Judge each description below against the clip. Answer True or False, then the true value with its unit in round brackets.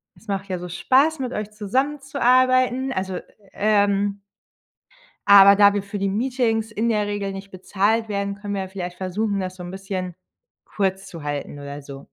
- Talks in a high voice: True (200 Hz)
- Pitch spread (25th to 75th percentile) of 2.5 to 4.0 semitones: True (2.8 semitones)